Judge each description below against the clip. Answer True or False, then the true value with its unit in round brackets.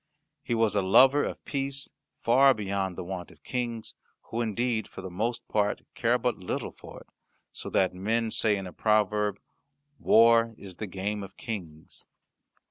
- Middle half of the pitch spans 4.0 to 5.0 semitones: False (3.4 semitones)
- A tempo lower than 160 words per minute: False (170 wpm)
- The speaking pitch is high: False (110 Hz)